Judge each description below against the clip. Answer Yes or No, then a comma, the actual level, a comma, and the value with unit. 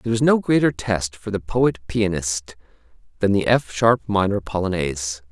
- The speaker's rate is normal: Yes, average, 170 wpm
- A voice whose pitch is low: Yes, low, 100 Hz